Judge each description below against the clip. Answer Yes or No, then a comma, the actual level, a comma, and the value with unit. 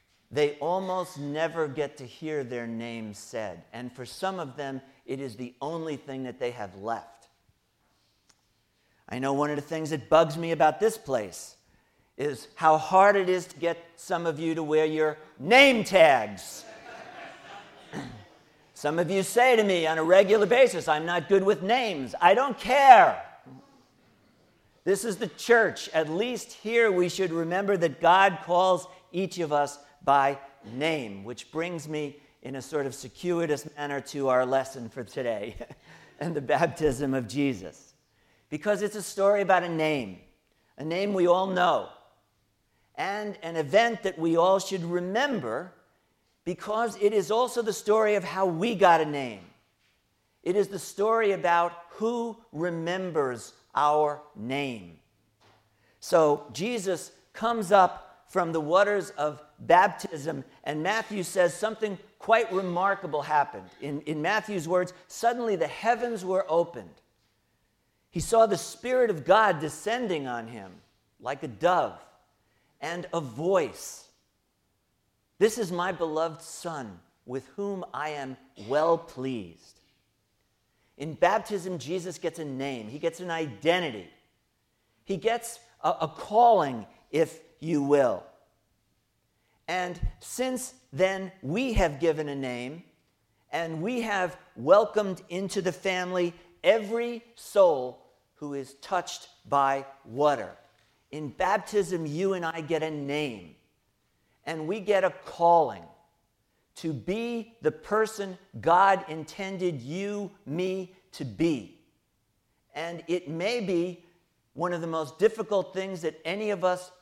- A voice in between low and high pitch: Yes, medium, 170 Hz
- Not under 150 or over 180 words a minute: No, average, 140 wpm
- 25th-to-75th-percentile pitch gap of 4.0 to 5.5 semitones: Yes, average, 5.2 semitones